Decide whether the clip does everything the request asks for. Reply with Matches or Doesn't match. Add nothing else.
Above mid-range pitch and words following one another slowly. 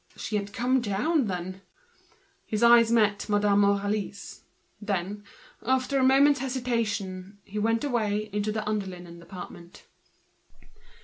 Matches